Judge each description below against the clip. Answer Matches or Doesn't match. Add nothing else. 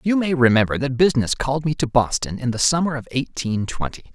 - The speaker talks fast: Matches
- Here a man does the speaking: Matches